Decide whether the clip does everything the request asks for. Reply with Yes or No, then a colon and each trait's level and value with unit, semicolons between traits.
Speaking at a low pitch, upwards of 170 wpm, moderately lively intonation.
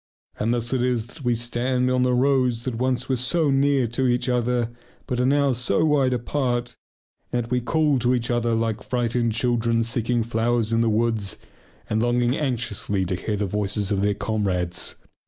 No: low, 120 Hz; average, 190 wpm; narrow, 1.9 semitones